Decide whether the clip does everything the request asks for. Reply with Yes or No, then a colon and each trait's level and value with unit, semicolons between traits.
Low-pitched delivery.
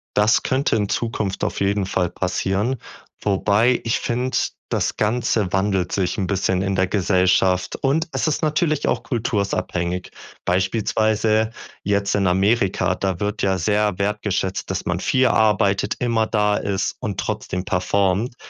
Yes: low, 100 Hz